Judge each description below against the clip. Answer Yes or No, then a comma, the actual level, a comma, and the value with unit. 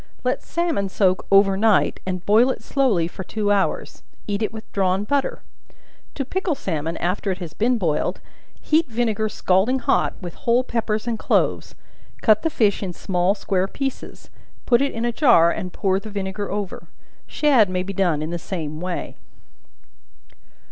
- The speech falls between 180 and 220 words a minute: No, average, 170 wpm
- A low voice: No, high, 205 Hz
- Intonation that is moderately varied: Yes, average, 4.3 semitones